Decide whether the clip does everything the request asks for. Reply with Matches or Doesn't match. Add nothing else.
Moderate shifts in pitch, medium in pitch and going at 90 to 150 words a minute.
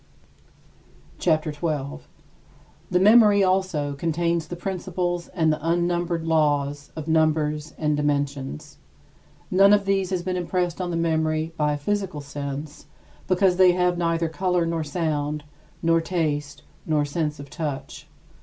Matches